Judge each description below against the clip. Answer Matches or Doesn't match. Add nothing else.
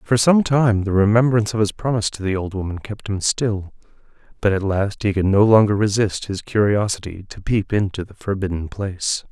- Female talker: Doesn't match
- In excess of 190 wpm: Matches